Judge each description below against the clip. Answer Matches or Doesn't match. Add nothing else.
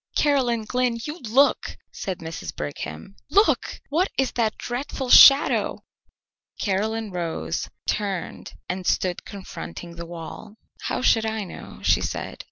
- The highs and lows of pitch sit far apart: Matches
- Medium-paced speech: Doesn't match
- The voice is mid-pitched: Doesn't match